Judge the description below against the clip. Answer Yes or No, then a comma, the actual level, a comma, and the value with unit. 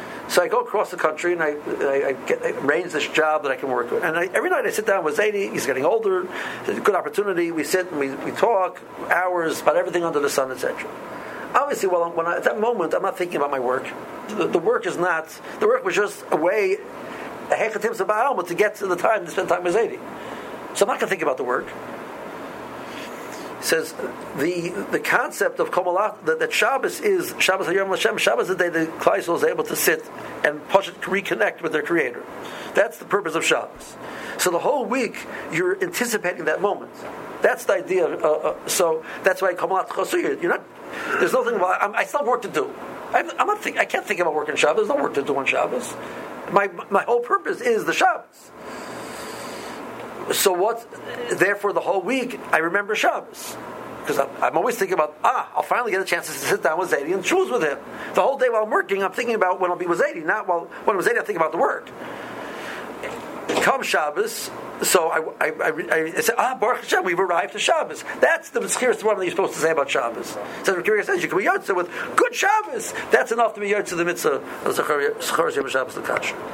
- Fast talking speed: Yes, fast, 225 wpm